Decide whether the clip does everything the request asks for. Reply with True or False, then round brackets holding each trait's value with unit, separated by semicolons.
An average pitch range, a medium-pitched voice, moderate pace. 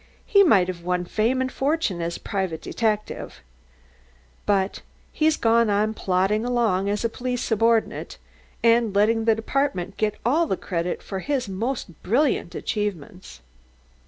False (4.1 semitones; 215 Hz; 145 wpm)